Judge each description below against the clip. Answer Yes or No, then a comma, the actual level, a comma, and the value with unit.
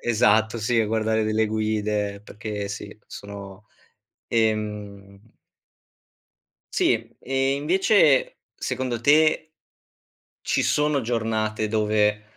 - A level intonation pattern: No, average, 3.0 semitones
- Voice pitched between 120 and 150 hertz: No, low, 110 Hz